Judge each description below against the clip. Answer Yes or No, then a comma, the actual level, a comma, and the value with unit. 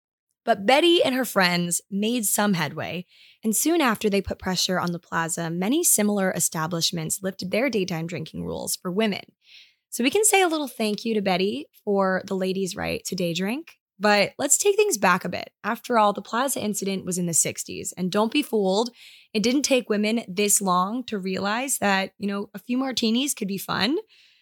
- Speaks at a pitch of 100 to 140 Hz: No, high, 205 Hz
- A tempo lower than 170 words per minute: No, average, 200 wpm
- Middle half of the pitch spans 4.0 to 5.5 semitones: Yes, average, 4.5 semitones